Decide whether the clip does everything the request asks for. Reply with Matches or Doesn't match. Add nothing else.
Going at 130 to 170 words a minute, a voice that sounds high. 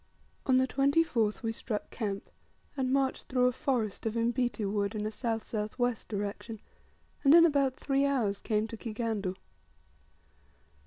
Matches